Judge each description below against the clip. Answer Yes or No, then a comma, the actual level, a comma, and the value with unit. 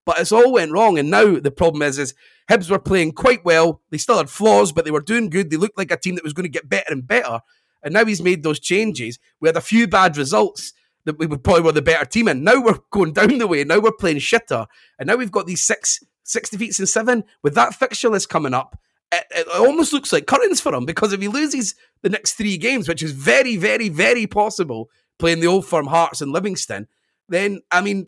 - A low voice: No, high, 190 Hz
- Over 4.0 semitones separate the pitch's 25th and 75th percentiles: Yes, average, 5.1 semitones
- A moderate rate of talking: No, fast, 250 wpm